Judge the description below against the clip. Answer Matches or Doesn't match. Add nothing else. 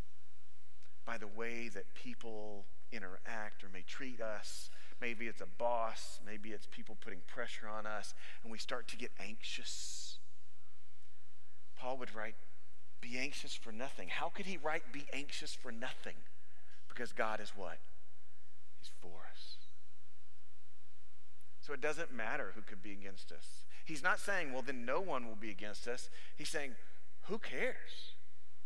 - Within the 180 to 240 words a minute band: Doesn't match